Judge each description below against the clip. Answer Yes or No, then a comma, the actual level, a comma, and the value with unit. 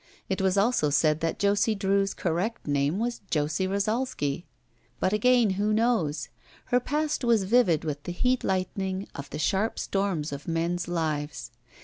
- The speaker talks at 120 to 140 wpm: No, average, 155 wpm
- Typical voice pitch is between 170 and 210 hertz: Yes, high, 190 Hz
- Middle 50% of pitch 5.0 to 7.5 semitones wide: Yes, wide, 5.6 semitones